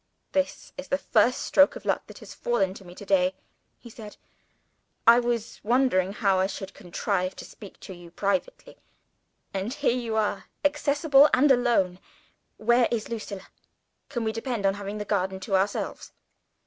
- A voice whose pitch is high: Yes, high, 215 Hz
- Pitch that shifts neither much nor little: Yes, average, 4.2 semitones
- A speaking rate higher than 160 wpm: Yes, average, 170 wpm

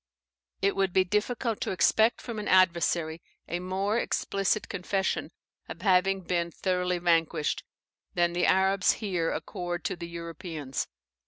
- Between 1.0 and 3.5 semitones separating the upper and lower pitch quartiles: Yes, narrow, 2.4 semitones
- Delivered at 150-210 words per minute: No, average, 140 wpm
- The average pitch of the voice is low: No, medium, 180 Hz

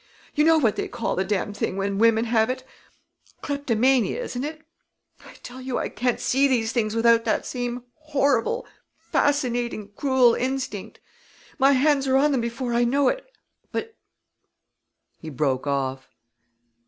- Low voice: No, high, 245 Hz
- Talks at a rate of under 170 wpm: Yes, average, 155 wpm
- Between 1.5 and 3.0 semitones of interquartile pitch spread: No, average, 3.7 semitones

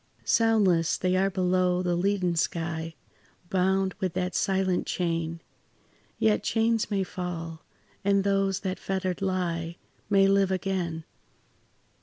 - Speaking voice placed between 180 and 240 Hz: Yes, medium, 185 Hz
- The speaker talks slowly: Yes, slow, 120 wpm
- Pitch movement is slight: Yes, narrow, 2.2 semitones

